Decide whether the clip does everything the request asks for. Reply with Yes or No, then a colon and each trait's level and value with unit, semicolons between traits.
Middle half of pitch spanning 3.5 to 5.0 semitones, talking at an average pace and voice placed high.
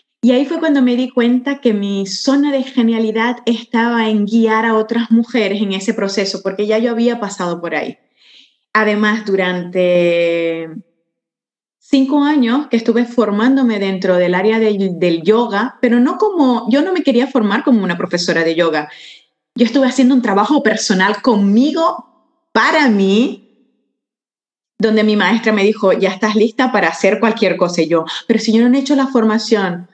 Yes: average, 4.3 semitones; average, 170 wpm; high, 225 Hz